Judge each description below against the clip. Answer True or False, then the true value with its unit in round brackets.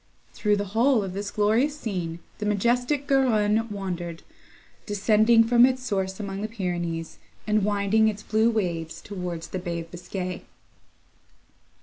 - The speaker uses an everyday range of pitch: True (3.6 semitones)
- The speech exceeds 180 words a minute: False (140 wpm)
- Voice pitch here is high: True (205 Hz)